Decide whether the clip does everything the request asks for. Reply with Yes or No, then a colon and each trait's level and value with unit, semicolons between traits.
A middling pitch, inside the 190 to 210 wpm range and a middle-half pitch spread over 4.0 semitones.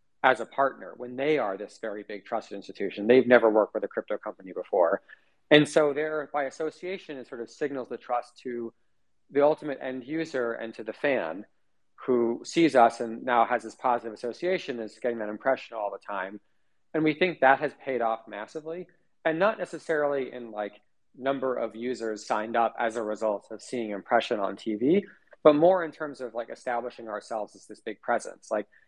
No: low, 125 Hz; average, 195 wpm; average, 4.9 semitones